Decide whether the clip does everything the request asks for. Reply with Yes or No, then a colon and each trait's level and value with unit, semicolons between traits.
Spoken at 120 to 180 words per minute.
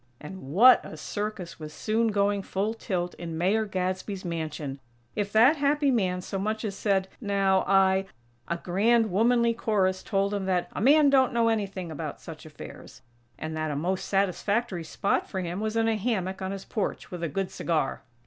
No: average, 190 wpm